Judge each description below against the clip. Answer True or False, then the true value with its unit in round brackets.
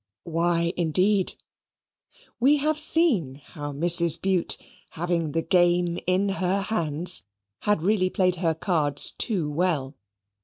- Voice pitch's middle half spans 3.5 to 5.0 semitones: False (2.9 semitones)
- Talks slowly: True (120 wpm)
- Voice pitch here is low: False (175 Hz)